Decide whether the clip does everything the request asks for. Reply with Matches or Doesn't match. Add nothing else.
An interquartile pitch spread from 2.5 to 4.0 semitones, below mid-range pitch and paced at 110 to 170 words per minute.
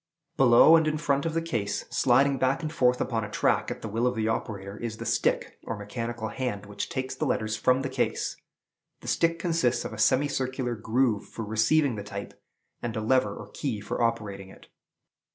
Doesn't match